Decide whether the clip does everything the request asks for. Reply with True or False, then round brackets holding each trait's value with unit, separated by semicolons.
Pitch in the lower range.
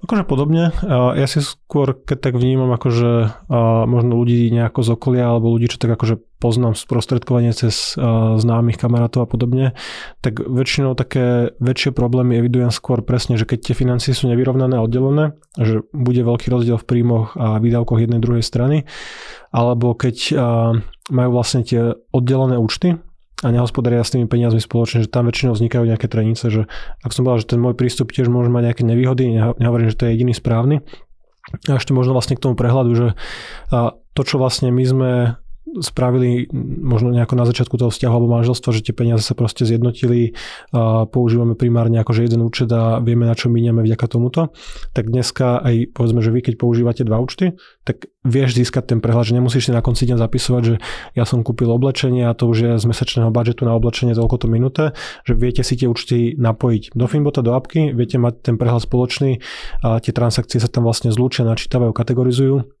True (120 Hz)